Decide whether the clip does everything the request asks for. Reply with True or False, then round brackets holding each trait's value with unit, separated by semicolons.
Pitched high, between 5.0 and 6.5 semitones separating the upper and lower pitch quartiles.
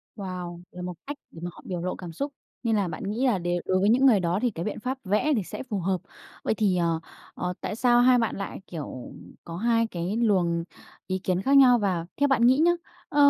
True (200 Hz; 5.3 semitones)